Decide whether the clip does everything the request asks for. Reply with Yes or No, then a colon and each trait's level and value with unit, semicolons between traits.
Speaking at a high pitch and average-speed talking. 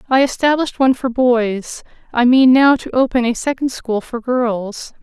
Yes: very high, 250 Hz; average, 180 wpm